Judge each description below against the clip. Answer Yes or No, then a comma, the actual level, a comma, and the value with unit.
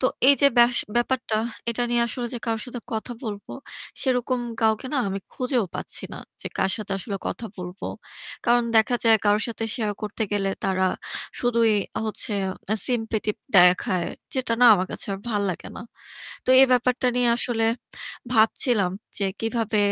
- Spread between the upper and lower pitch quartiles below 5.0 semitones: Yes, average, 2.9 semitones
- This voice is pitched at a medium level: No, high, 225 Hz